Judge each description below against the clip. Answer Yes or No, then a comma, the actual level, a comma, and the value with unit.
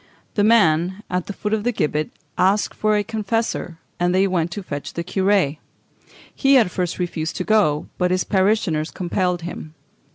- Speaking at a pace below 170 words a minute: No, average, 175 wpm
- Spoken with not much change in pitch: No, average, 3.6 semitones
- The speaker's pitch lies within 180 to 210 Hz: Yes, medium, 185 Hz